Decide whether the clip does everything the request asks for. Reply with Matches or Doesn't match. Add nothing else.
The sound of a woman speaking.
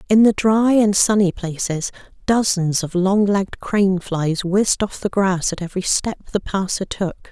Matches